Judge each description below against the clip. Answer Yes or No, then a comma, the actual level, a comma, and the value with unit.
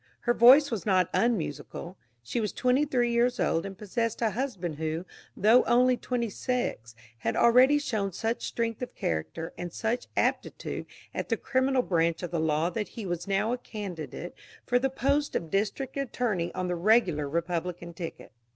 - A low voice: No, high, 210 Hz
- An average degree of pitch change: No, wide, 6.2 semitones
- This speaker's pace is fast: No, average, 175 wpm